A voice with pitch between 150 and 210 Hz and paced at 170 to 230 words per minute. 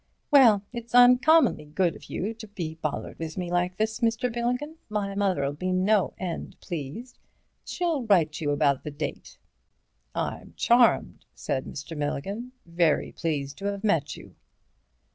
No: high, 190 Hz; average, 150 wpm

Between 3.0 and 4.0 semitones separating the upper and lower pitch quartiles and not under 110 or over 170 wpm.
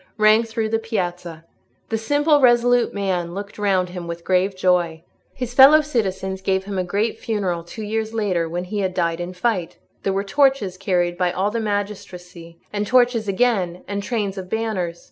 No: average, 3.7 semitones; average, 185 wpm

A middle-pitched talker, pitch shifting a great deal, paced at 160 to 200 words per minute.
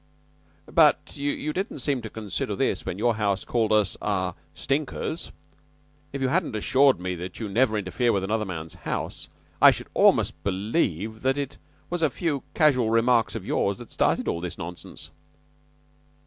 No: low, 110 Hz; wide, 5.7 semitones; average, 165 wpm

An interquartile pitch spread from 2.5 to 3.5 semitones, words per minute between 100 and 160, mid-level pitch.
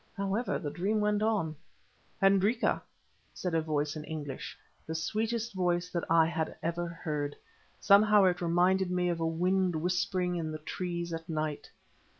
Yes: average, 3.1 semitones; average, 155 wpm; medium, 175 Hz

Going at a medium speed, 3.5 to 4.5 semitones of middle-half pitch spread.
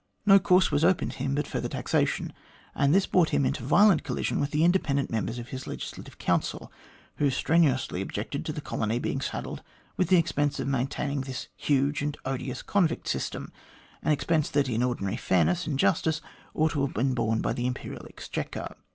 Yes: average, 190 wpm; average, 3.8 semitones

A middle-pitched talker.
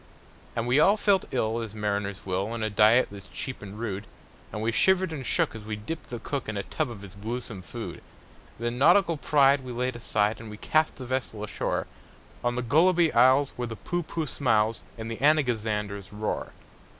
No: low, 115 Hz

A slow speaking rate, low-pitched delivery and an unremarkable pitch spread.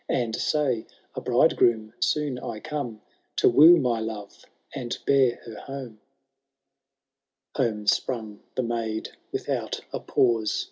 Yes: slow, 130 wpm; low, 120 Hz; average, 3.4 semitones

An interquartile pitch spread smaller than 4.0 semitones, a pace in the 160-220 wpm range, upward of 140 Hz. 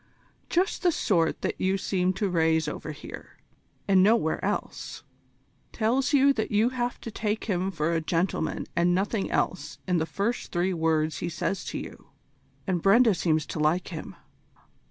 No: average, 4.8 semitones; average, 170 wpm; medium, 185 Hz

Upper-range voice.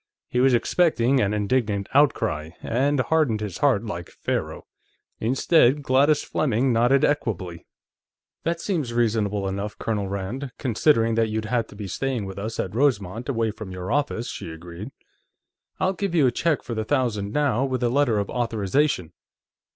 No: low, 115 Hz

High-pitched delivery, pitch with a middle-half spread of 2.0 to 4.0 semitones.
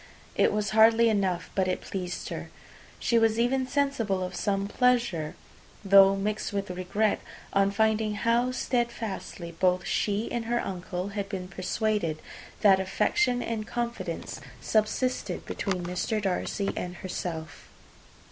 Yes: high, 205 Hz; average, 3.7 semitones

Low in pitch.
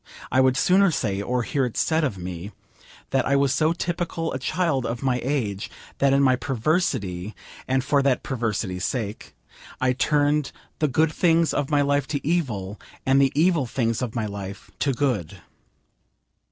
Yes: low, 130 Hz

